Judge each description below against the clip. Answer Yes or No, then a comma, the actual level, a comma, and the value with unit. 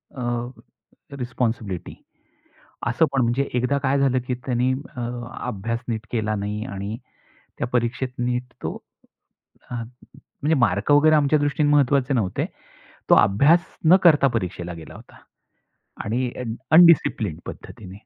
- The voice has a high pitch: No, low, 125 Hz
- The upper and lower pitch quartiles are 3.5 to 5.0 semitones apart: Yes, average, 4.1 semitones